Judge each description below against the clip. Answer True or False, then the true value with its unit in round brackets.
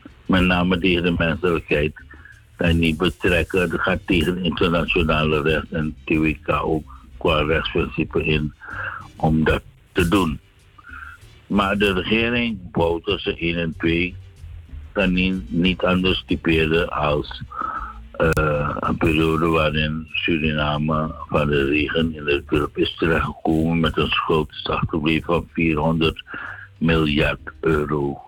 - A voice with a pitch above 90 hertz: False (80 Hz)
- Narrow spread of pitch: True (2.0 semitones)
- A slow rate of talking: True (120 wpm)